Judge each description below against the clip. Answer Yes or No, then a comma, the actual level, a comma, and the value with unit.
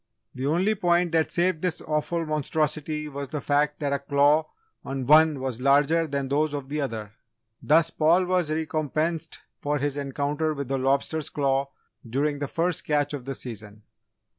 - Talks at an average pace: Yes, average, 170 wpm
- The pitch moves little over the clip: Yes, narrow, 2.3 semitones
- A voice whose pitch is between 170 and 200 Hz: No, medium, 150 Hz